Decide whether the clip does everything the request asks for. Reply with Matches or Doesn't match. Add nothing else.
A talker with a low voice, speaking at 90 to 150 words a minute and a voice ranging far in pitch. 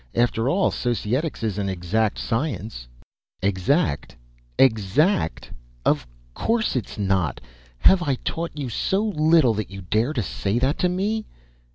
Matches